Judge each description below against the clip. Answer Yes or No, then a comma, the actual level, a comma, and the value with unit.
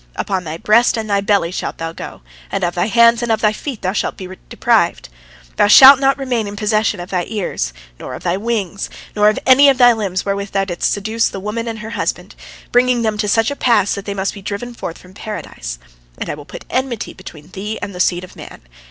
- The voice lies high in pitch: Yes, high, 210 Hz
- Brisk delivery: Yes, fast, 235 wpm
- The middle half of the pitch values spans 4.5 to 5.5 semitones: No, average, 3.7 semitones